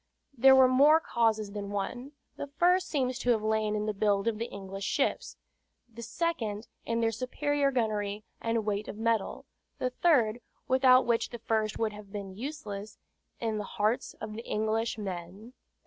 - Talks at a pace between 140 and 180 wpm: Yes, average, 175 wpm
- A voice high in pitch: Yes, high, 225 Hz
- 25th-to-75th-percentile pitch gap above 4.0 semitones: No, average, 3.3 semitones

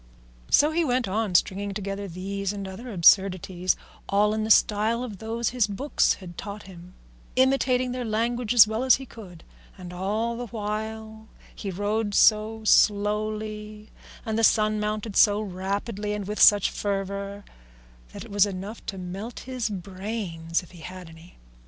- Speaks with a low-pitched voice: No, high, 210 Hz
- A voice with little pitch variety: Yes, narrow, 2.3 semitones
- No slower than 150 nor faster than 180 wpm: Yes, average, 165 wpm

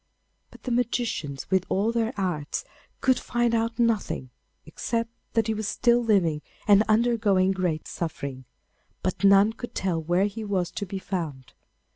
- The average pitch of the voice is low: No, high, 200 Hz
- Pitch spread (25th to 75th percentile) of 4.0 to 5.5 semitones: Yes, average, 4.7 semitones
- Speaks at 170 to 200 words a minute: No, average, 155 wpm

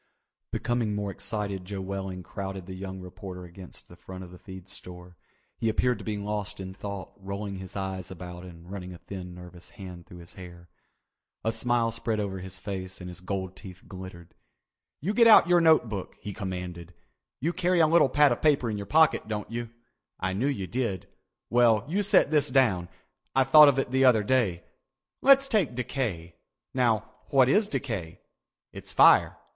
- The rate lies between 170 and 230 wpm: Yes, average, 185 wpm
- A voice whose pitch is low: Yes, low, 100 Hz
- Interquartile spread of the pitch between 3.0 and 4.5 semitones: No, average, 5.1 semitones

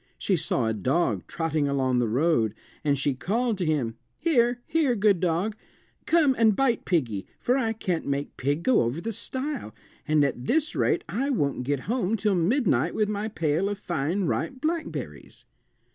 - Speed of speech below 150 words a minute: No, average, 175 wpm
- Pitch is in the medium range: Yes, medium, 180 Hz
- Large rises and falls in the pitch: Yes, wide, 8.6 semitones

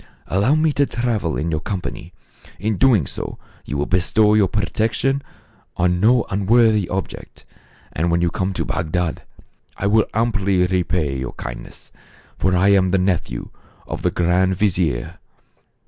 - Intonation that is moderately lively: Yes, average, 3.7 semitones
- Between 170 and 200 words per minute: No, average, 150 wpm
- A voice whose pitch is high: No, very low, 95 Hz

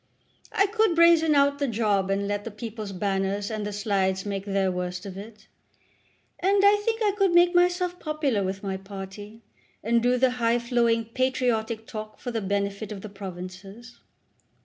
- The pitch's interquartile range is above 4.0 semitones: Yes, wide, 5.4 semitones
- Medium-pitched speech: No, high, 220 Hz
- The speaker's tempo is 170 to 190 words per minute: Yes, average, 175 wpm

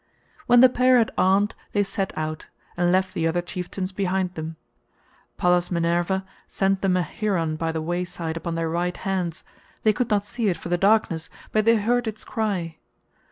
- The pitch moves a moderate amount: Yes, average, 3.3 semitones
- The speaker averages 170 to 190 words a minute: Yes, average, 185 wpm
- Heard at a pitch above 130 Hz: Yes, medium, 185 Hz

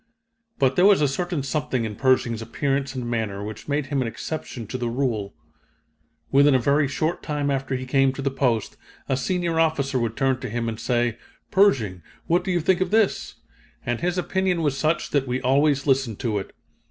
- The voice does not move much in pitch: No, average, 4.2 semitones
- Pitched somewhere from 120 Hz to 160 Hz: Yes, low, 135 Hz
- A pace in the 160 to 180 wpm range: No, average, 200 wpm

